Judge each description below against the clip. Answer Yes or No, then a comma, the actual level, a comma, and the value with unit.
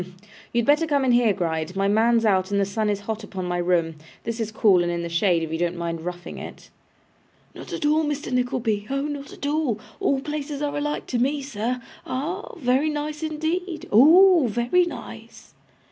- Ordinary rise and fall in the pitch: No, wide, 7.1 semitones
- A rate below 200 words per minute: No, fast, 205 wpm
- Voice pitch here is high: Yes, high, 240 Hz